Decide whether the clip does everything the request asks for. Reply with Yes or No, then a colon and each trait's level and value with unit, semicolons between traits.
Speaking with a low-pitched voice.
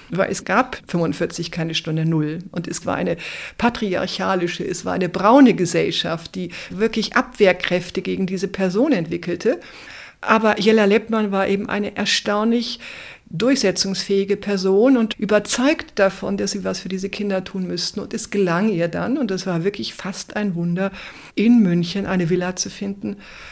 No: high, 195 Hz